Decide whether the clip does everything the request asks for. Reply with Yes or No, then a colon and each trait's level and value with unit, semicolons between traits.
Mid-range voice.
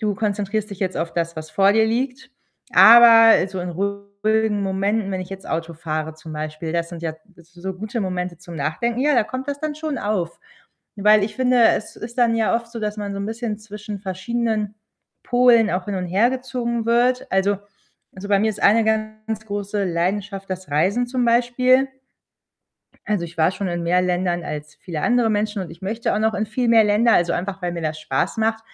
No: high, 205 Hz